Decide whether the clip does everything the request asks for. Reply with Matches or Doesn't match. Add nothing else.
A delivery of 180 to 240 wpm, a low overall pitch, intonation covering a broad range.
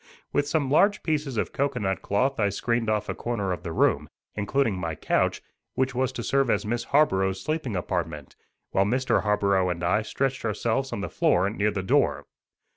Matches